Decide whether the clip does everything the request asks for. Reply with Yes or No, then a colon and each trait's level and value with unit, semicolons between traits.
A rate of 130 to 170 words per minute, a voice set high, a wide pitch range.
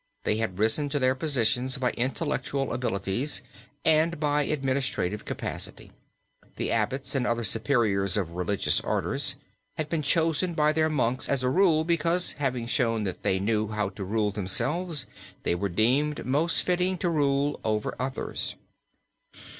No: average, 150 wpm; low, 130 Hz; wide, 5.8 semitones